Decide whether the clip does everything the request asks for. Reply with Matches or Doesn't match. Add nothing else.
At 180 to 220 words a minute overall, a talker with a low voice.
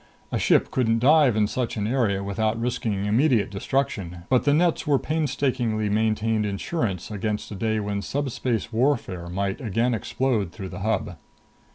Doesn't match